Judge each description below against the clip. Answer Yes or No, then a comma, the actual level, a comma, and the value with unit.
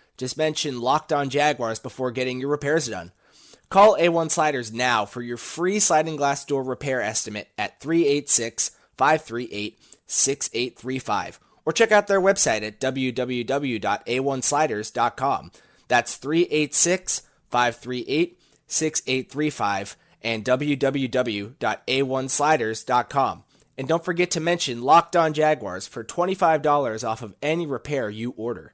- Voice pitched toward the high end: No, low, 135 Hz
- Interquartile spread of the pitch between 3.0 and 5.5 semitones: Yes, average, 4.2 semitones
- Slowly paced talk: Yes, slow, 115 wpm